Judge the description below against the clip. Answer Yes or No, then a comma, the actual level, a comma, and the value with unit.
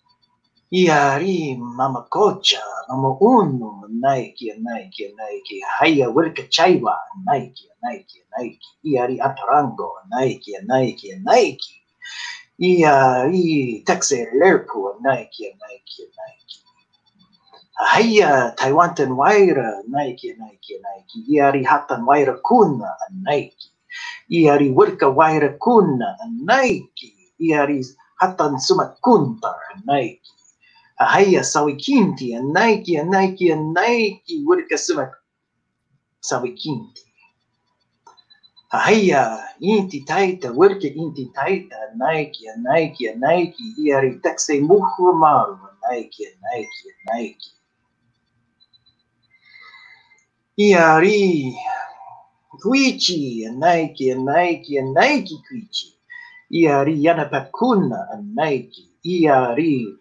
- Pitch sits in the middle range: Yes, medium, 165 Hz